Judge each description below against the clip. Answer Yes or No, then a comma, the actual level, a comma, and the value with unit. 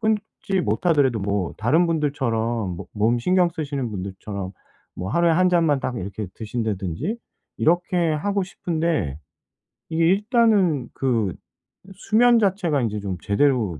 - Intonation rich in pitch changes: Yes, wide, 8.9 semitones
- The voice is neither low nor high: Yes, medium, 145 Hz